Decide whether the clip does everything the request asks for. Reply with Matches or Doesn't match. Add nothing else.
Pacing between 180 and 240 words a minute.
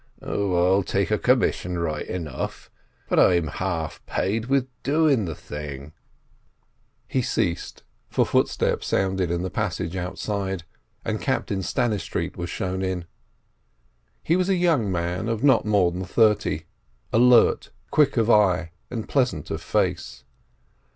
Doesn't match